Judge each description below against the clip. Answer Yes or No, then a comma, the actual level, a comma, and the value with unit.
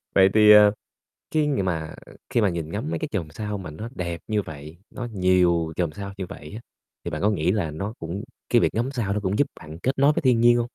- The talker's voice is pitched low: Yes, low, 100 Hz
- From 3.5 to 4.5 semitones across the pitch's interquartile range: No, average, 5.0 semitones